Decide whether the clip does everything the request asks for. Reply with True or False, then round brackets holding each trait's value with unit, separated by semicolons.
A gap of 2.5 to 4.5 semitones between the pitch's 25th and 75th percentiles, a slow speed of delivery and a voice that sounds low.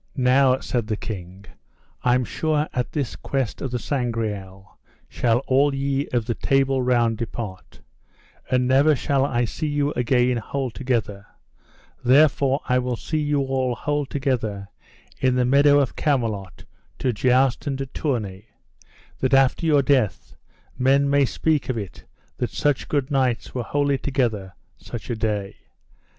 False (3.2 semitones; 155 wpm; 130 Hz)